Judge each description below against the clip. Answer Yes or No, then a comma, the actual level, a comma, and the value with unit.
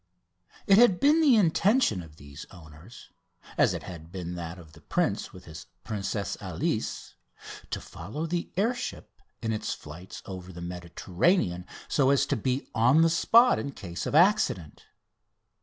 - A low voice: Yes, low, 100 Hz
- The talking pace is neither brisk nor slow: Yes, average, 160 wpm